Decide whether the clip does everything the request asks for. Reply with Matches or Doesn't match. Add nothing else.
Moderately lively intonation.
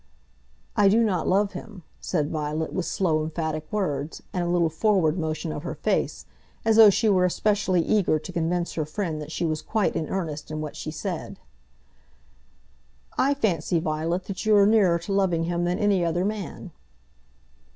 Matches